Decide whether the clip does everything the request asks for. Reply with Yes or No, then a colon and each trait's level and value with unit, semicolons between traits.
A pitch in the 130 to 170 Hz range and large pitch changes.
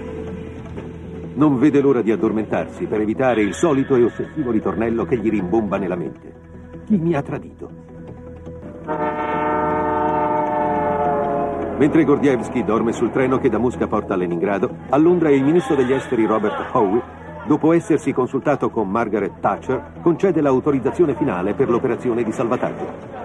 Yes: medium, 140 Hz; wide, 8.4 semitones